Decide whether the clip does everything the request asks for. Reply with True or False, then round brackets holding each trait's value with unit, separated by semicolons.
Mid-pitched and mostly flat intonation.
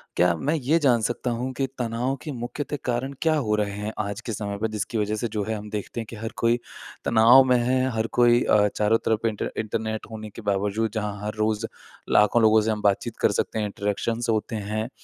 False (110 Hz; 2.3 semitones)